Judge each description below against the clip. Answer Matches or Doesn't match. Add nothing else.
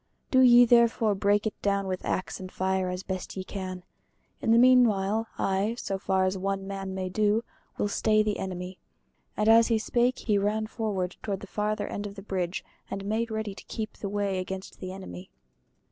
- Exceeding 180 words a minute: Matches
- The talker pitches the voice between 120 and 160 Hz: Doesn't match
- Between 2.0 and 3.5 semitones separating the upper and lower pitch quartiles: Matches